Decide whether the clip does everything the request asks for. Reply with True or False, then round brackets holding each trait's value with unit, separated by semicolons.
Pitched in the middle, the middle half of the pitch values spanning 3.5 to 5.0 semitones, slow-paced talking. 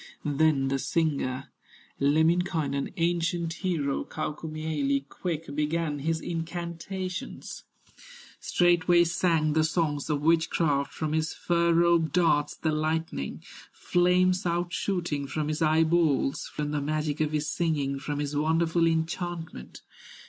False (160 Hz; 2.5 semitones; 120 wpm)